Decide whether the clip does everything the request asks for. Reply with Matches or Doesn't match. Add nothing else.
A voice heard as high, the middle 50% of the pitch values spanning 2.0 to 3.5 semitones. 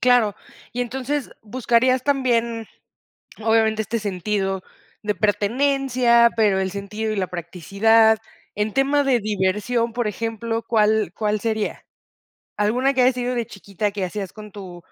Matches